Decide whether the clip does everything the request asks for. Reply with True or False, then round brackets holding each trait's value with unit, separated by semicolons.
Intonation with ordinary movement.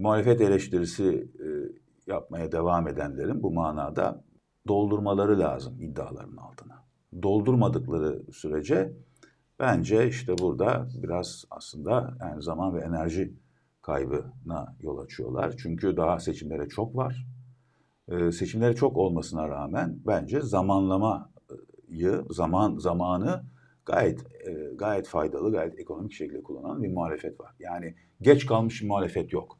False (5.9 semitones)